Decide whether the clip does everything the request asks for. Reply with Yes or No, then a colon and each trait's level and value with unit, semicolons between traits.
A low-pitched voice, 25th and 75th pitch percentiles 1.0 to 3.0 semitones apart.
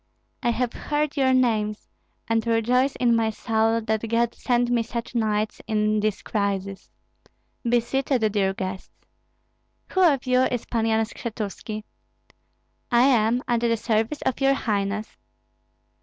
No: high, 230 Hz; narrow, 2.4 semitones